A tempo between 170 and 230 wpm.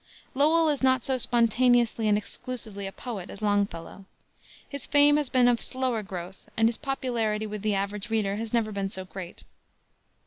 Yes: average, 175 wpm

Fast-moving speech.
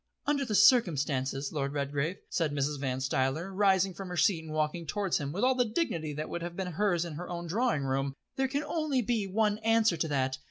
Yes: fast, 225 wpm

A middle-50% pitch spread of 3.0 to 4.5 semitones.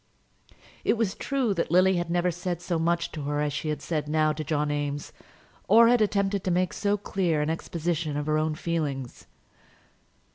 Yes: average, 3.6 semitones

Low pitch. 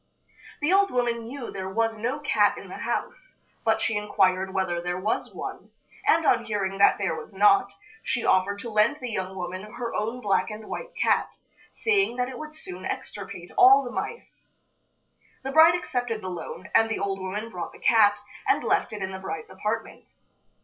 No: high, 215 Hz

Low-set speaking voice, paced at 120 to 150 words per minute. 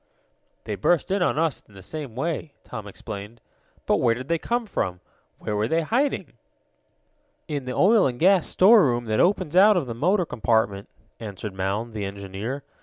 No: low, 125 Hz; average, 180 wpm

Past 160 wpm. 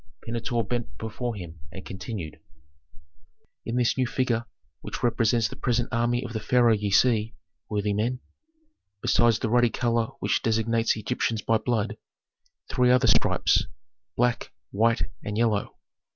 No: average, 140 wpm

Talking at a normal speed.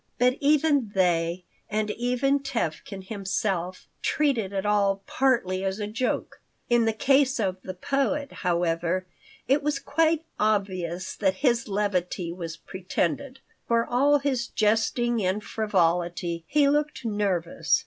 No: slow, 130 wpm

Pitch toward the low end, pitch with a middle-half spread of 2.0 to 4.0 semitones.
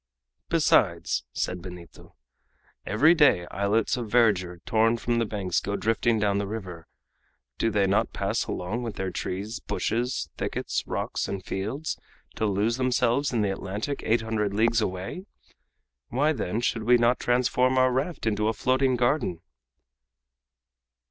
Yes: low, 110 Hz; average, 3.7 semitones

